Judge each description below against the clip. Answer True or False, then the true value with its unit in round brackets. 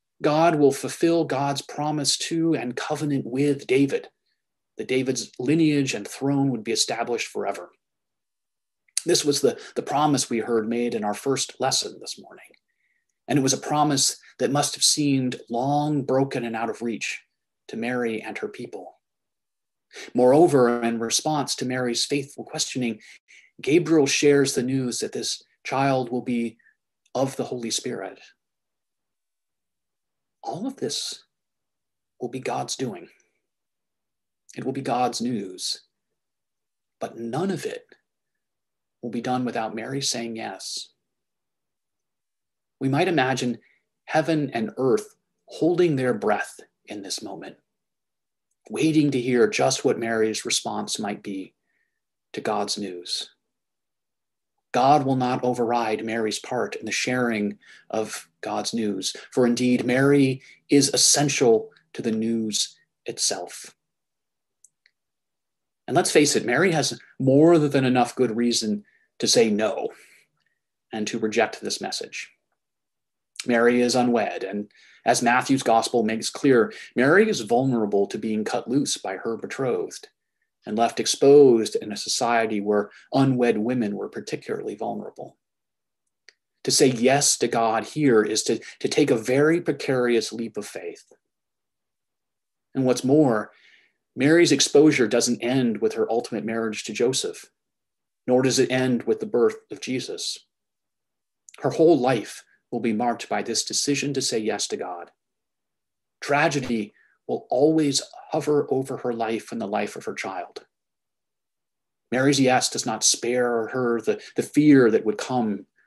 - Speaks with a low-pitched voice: True (130 Hz)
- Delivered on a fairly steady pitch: False (3.8 semitones)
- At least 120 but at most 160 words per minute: True (140 wpm)